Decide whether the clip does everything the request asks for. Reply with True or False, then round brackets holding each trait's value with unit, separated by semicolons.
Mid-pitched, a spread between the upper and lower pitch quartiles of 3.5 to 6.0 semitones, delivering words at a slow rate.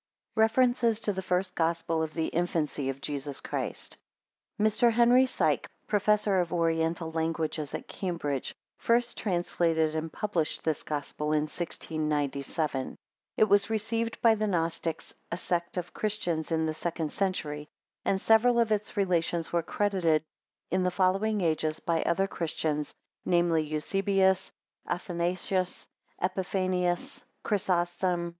True (175 Hz; 3.9 semitones; 130 wpm)